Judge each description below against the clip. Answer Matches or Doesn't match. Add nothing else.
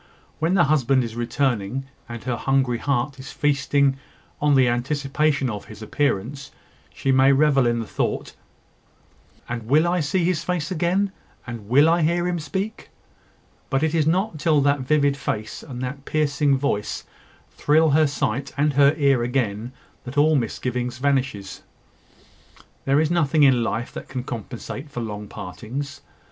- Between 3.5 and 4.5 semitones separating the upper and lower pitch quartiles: Matches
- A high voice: Doesn't match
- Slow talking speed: Doesn't match